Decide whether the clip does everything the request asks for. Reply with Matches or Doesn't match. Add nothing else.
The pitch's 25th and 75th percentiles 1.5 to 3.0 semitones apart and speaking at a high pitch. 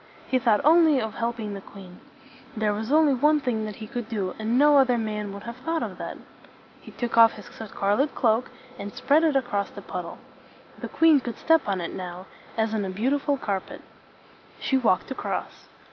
Doesn't match